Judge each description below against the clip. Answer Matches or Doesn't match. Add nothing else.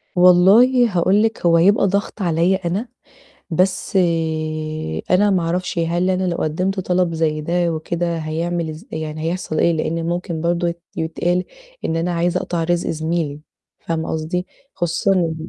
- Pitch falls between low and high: Matches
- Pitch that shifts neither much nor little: Doesn't match